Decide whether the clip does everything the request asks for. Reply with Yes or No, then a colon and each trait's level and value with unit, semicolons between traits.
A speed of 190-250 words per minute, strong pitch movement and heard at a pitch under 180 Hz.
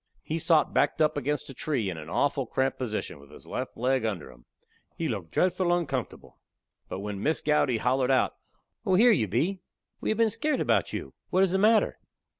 Yes: fast, 205 wpm; wide, 7.9 semitones; low, 135 Hz